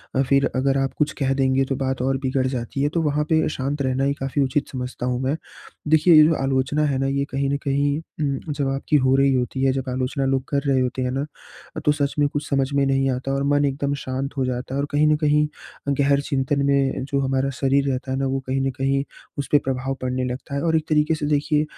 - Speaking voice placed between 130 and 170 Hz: Yes, low, 135 Hz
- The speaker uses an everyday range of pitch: No, narrow, 1.3 semitones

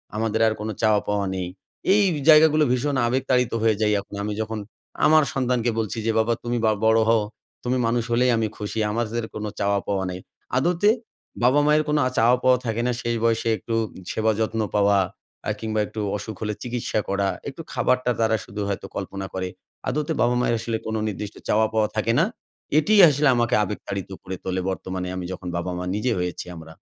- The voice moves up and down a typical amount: Yes, average, 3.2 semitones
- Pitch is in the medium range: No, low, 110 Hz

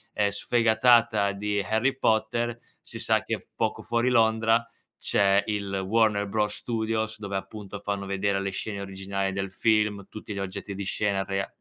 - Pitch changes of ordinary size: No, narrow, 2.1 semitones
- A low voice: Yes, low, 105 Hz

